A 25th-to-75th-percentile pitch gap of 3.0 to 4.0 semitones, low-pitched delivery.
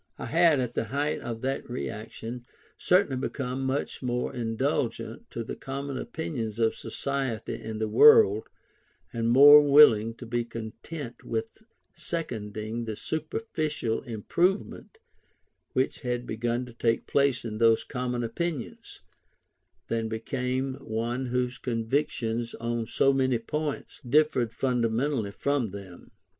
Yes: average, 3.5 semitones; low, 125 Hz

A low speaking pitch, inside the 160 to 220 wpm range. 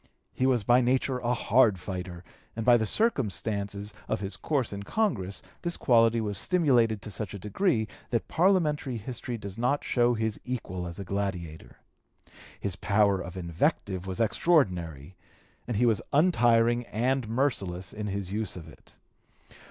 Yes: low, 110 Hz; average, 165 wpm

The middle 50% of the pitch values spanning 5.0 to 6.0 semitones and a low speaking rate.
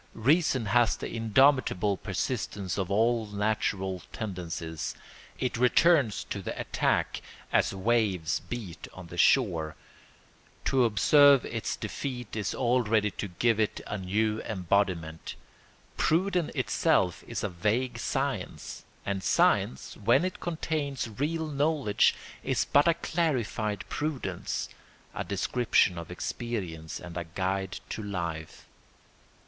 Yes: wide, 5.5 semitones; slow, 120 wpm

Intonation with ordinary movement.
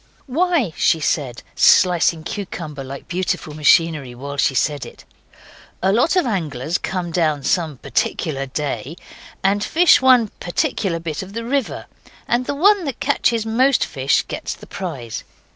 No: wide, 7.9 semitones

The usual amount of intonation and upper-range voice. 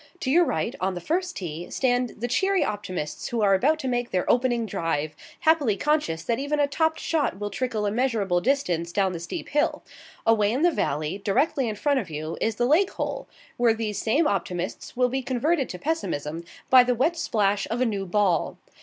No: wide, 6.7 semitones; high, 230 Hz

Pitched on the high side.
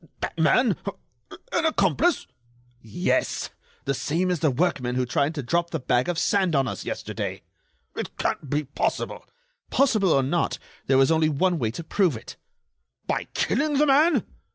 No: medium, 160 Hz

